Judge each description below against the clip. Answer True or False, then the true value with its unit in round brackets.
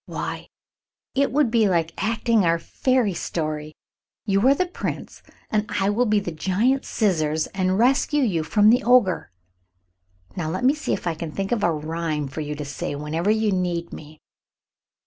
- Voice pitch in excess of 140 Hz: True (190 Hz)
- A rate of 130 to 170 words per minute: False (180 wpm)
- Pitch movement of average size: False (6.2 semitones)